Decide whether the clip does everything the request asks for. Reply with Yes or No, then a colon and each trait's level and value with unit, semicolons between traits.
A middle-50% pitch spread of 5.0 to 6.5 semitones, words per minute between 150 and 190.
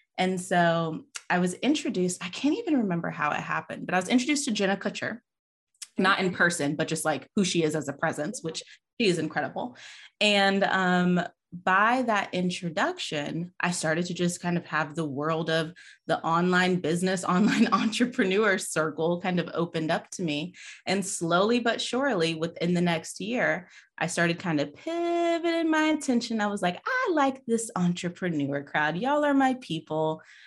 Yes: wide, 5.6 semitones; average, 175 wpm